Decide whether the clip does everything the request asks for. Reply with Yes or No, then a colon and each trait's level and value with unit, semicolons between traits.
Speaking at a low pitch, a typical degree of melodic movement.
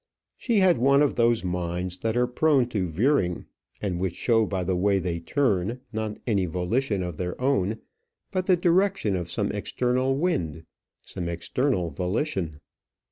No: low, 105 Hz; wide, 6.9 semitones